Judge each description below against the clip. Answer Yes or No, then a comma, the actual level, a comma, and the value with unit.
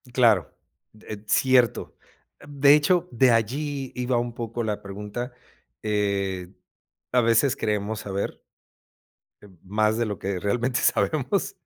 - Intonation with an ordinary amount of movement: Yes, average, 3.6 semitones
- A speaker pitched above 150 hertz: No, low, 115 Hz